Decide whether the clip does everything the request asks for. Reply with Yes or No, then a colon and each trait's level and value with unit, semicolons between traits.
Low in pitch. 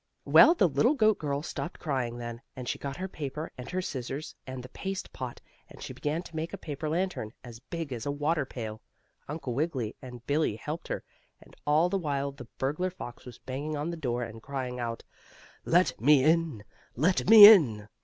No: medium, 145 Hz